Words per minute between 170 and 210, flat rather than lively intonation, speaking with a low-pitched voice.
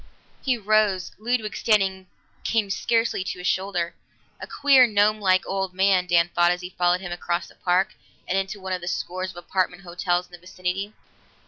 No: average, 185 wpm; narrow, 2.2 semitones; medium, 185 Hz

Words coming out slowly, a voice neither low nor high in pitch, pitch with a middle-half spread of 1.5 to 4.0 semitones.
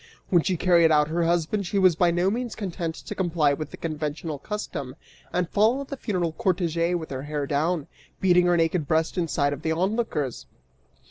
No: average, 195 wpm; medium, 170 Hz; average, 3.2 semitones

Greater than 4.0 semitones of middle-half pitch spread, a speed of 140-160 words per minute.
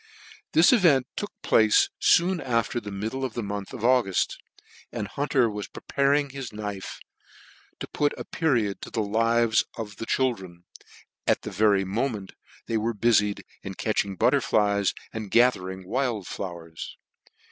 Yes: average, 4.4 semitones; average, 150 wpm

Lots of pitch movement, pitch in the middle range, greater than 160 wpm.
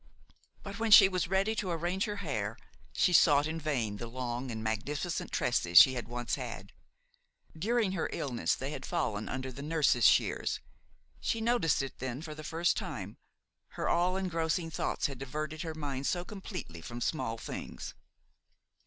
Yes: wide, 6.3 semitones; medium, 155 Hz; average, 170 wpm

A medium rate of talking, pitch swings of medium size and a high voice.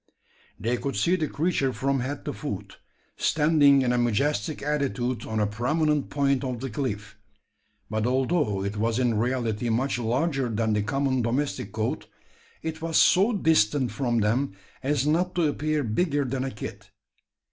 No: average, 165 wpm; average, 4.3 semitones; low, 130 Hz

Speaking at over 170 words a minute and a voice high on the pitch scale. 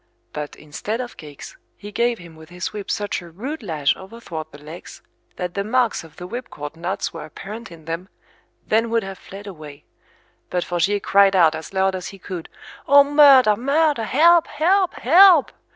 Yes: average, 185 wpm; high, 195 Hz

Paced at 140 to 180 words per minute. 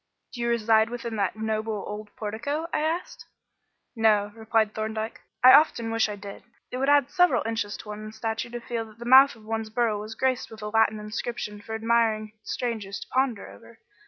No: average, 195 wpm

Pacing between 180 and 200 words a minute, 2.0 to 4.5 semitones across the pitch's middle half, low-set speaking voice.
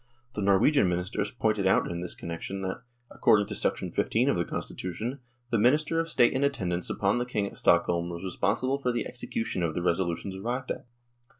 No: average, 195 wpm; wide, 5.5 semitones; low, 100 Hz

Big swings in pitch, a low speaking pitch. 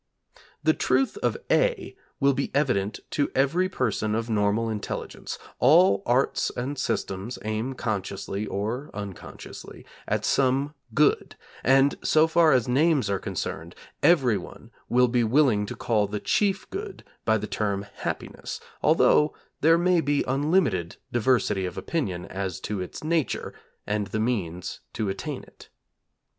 Yes: wide, 6.1 semitones; low, 125 Hz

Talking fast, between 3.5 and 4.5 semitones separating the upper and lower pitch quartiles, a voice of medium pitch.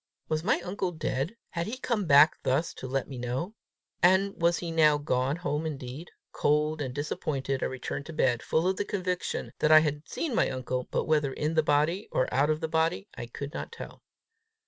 Yes: fast, 210 wpm; average, 3.8 semitones; medium, 155 Hz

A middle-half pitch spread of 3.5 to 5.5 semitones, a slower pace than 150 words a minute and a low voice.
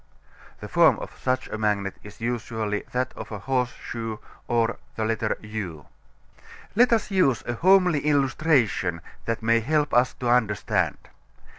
Yes: average, 3.9 semitones; average, 140 wpm; low, 115 Hz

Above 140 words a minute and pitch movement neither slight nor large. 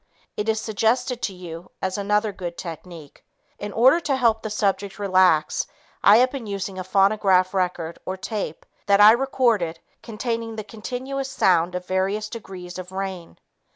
Yes: average, 160 wpm; average, 3.4 semitones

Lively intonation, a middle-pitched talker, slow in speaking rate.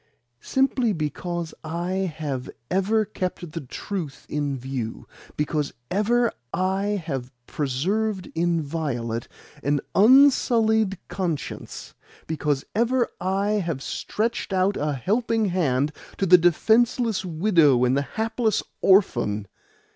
Yes: wide, 6.5 semitones; medium, 180 Hz; slow, 110 wpm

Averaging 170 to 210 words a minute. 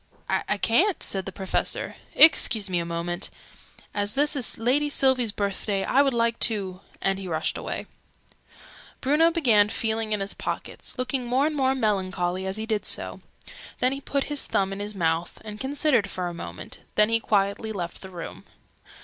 Yes: average, 185 wpm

